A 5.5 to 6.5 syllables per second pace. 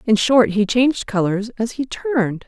No: 4.7 syllables/s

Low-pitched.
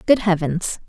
No: high, 190 Hz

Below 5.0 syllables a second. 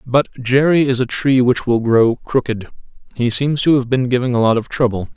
No: 5.2 syllables/s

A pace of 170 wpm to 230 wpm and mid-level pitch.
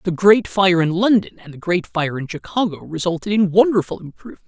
Yes: average, 200 wpm; medium, 180 Hz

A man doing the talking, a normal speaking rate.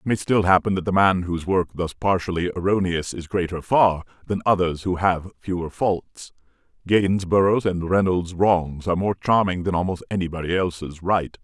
Yes: male; average, 175 wpm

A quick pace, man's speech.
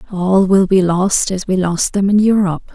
No: fast, 220 wpm; female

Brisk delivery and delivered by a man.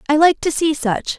No: fast, 250 wpm; female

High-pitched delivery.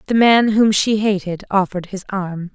Yes: high, 200 Hz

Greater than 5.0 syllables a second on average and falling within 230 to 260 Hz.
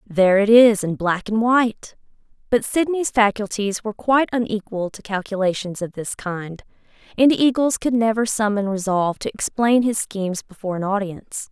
No: 5.3 syllables/s; high, 215 Hz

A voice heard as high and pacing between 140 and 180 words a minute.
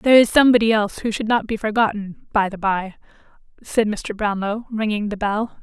No: high, 215 Hz; average, 190 wpm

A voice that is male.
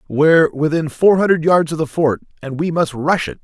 Yes: male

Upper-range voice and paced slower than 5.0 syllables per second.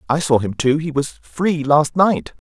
No: medium, 145 Hz; 4.1 syllables/s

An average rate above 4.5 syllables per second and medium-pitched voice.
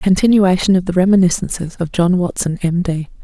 Yes: 5.9 syllables/s; medium, 180 Hz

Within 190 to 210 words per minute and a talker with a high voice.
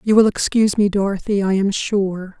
Yes: average, 200 wpm; high, 200 Hz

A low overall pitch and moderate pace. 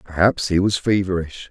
Yes: very low, 95 Hz; average, 160 wpm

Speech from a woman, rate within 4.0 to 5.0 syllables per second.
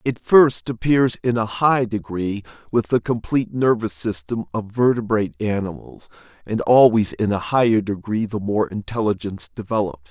No: male; 4.9 syllables/s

